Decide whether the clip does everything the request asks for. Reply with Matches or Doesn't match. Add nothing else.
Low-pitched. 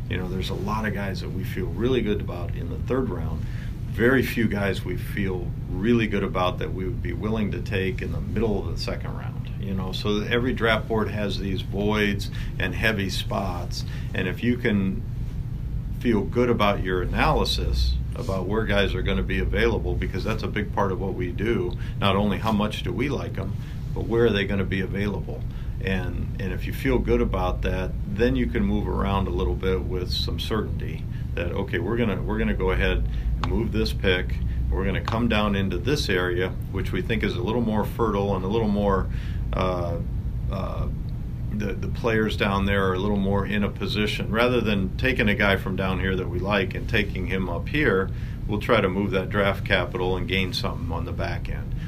Matches